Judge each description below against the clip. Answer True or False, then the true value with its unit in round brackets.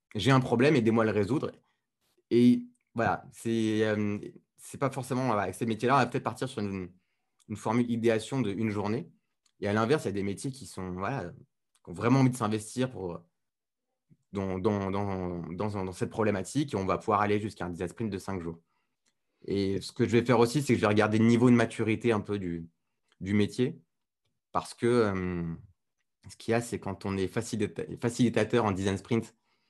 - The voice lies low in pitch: True (110 Hz)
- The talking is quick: False (210 wpm)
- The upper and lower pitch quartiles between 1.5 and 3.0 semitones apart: False (3.5 semitones)